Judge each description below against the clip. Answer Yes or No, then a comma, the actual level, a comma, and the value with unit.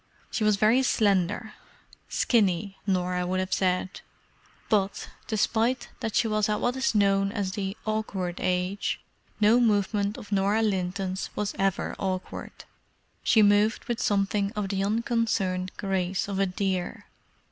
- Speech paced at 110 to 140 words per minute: Yes, slow, 135 wpm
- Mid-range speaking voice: No, high, 200 Hz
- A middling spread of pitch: No, narrow, 2.3 semitones